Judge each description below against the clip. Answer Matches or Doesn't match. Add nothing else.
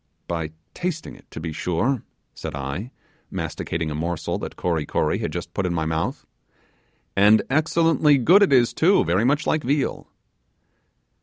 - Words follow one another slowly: Doesn't match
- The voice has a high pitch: Doesn't match